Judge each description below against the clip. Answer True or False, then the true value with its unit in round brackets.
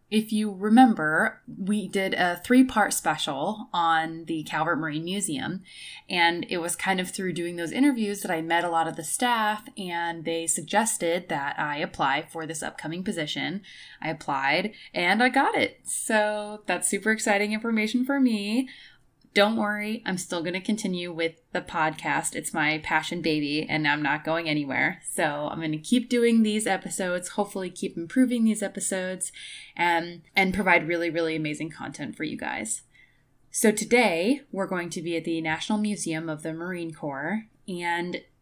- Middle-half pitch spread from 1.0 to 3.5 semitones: False (4.4 semitones)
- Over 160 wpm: True (175 wpm)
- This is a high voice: False (180 Hz)